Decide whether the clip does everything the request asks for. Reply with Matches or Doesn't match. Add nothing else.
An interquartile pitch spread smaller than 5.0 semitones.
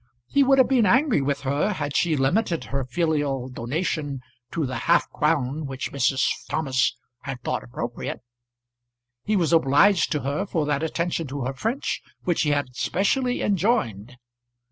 Doesn't match